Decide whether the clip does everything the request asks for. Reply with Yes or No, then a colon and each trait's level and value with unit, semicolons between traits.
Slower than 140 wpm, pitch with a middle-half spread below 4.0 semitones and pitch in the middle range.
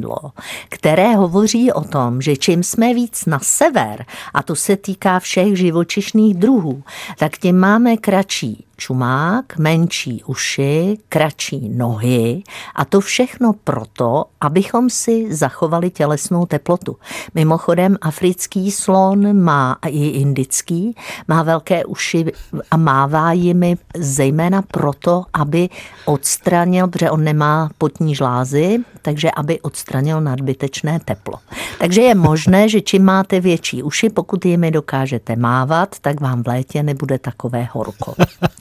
No: average, 125 wpm; average, 5.0 semitones; medium, 165 Hz